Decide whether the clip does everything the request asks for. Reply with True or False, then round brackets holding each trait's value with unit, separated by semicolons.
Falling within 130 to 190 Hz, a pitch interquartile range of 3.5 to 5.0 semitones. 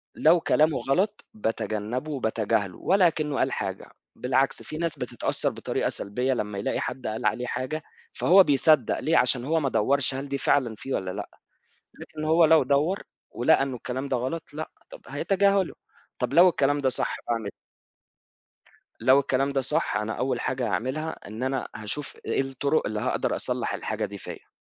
True (135 Hz; 4.3 semitones)